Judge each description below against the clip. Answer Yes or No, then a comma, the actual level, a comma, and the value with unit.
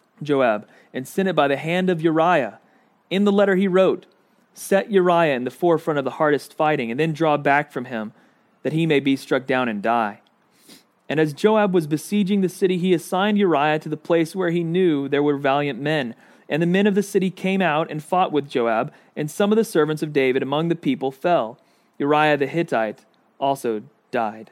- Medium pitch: Yes, medium, 160 Hz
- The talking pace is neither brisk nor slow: No, fast, 210 wpm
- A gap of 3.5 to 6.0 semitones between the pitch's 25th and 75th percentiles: Yes, average, 4.9 semitones